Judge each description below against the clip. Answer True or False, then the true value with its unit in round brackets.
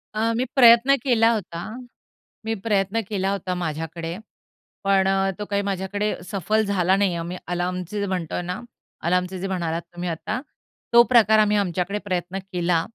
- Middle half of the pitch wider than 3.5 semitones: False (2.9 semitones)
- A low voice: False (190 Hz)